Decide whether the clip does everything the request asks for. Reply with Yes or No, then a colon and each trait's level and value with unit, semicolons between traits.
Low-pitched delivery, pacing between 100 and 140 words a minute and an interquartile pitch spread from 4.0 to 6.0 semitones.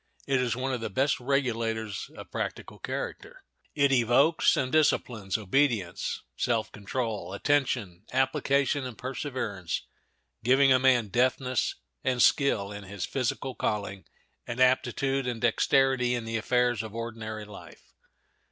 No: low, 125 Hz; slow, 135 wpm; average, 3.3 semitones